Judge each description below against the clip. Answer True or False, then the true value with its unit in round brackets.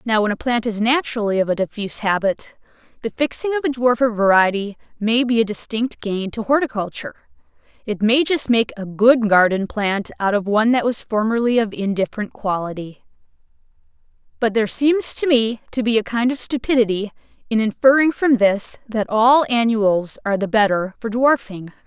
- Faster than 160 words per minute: True (170 wpm)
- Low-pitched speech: False (225 Hz)